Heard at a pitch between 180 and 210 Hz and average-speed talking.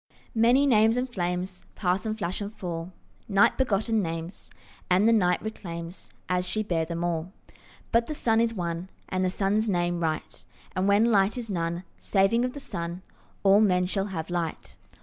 Yes: high, 190 Hz; average, 180 wpm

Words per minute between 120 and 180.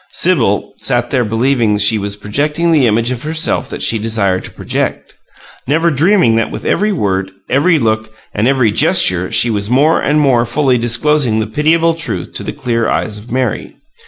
No: average, 190 wpm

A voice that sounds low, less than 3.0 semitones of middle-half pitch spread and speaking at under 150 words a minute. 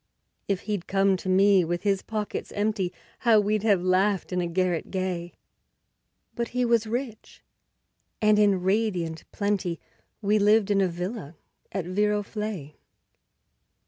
No: high, 200 Hz; narrow, 2.6 semitones; average, 140 wpm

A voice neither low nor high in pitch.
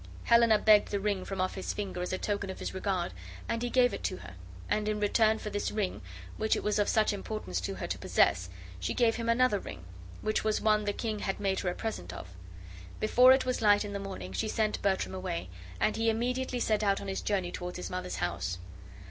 No: high, 205 Hz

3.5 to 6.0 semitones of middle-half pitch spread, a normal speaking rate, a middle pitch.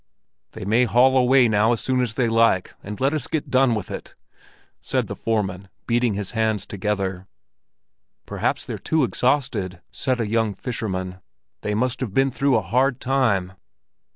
No: average, 4.0 semitones; average, 170 wpm; low, 115 Hz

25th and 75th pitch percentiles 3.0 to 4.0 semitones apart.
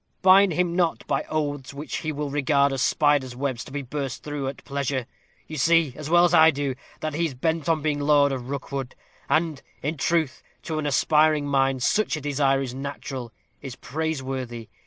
No: narrow, 2.6 semitones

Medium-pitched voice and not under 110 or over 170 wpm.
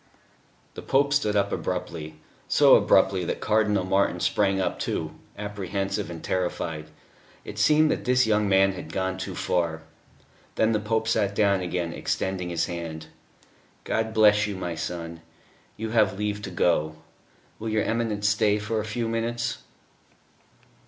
No: low, 100 Hz; average, 150 wpm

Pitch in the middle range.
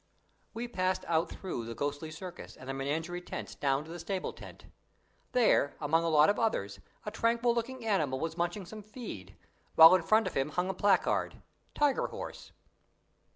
Yes: medium, 175 Hz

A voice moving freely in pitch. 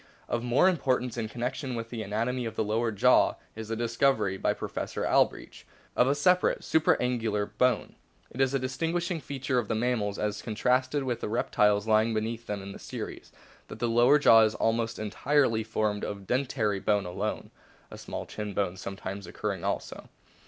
No: average, 3.2 semitones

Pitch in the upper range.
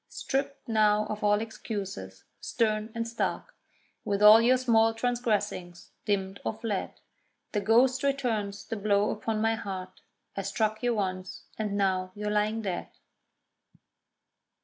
Yes: high, 215 Hz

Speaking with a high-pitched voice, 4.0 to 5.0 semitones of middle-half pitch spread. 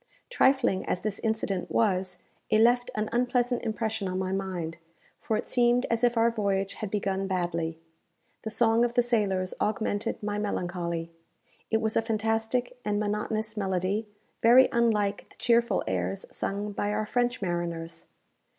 No: high, 210 Hz; average, 3.5 semitones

